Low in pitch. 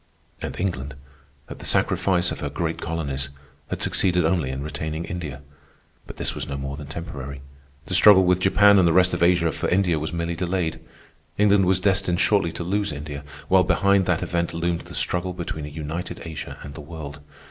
Yes: very low, 85 Hz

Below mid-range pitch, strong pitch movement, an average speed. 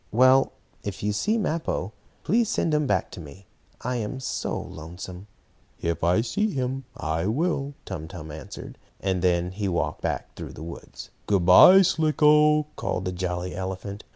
Yes: low, 100 Hz; wide, 8.1 semitones; average, 170 wpm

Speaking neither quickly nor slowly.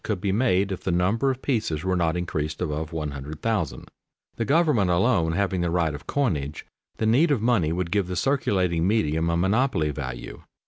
Yes: average, 185 wpm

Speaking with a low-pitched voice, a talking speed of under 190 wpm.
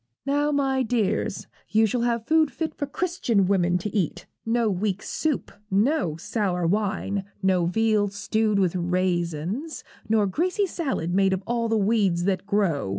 No: high, 210 Hz; average, 155 wpm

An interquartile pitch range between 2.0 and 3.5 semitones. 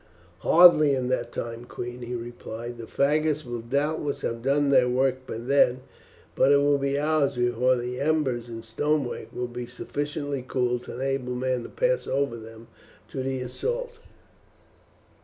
Yes: average, 2.9 semitones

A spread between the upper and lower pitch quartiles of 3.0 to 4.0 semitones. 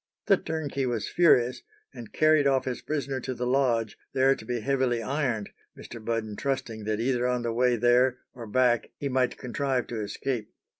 No: narrow, 2.6 semitones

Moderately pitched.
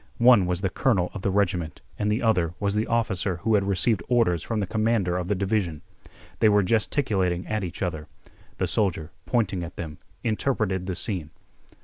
No: low, 100 Hz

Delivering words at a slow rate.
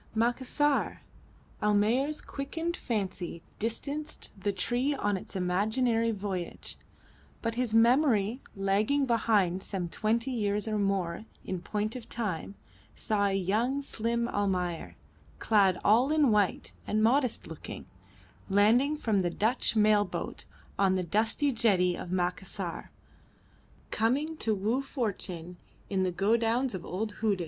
Yes: slow, 130 wpm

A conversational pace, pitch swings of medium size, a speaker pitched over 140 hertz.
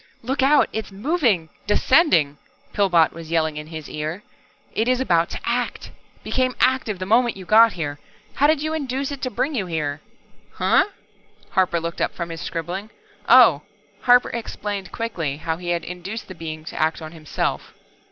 No: average, 175 wpm; wide, 7.2 semitones; high, 190 Hz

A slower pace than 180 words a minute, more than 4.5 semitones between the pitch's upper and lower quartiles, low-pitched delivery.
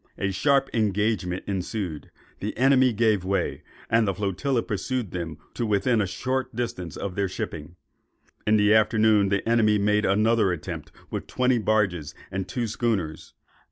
No: average, 155 wpm; average, 3.5 semitones; low, 105 Hz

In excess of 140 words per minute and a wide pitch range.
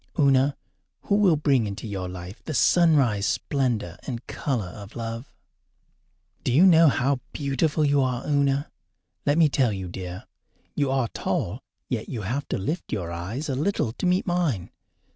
Yes: average, 165 wpm; wide, 5.8 semitones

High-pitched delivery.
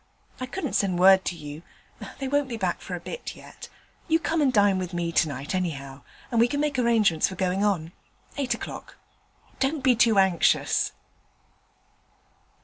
Yes: high, 195 Hz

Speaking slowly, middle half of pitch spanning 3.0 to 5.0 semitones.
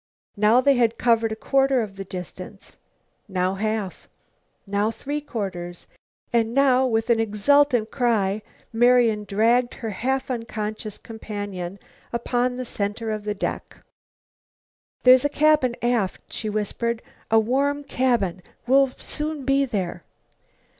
Yes: slow, 130 wpm; average, 3.6 semitones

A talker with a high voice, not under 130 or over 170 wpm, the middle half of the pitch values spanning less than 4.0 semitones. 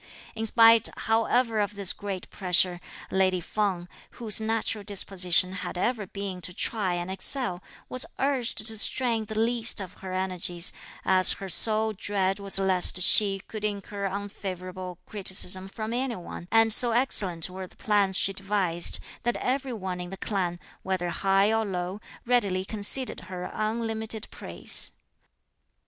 Yes: high, 200 Hz; average, 150 wpm; average, 3.1 semitones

